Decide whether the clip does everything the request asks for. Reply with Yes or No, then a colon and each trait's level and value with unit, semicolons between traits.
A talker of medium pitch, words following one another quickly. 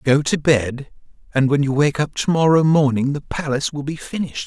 Yes: medium, 145 Hz; fast, 215 wpm